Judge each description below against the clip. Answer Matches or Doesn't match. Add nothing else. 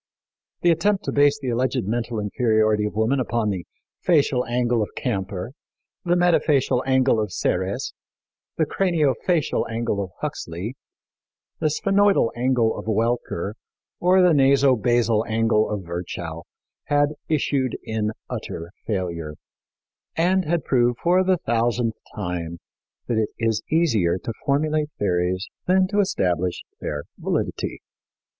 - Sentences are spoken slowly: Matches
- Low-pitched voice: Matches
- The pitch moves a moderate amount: Doesn't match